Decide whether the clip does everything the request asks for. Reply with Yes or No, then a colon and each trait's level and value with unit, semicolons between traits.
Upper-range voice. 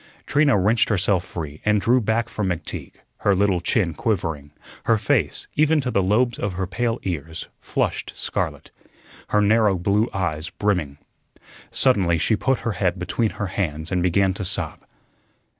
No: low, 100 Hz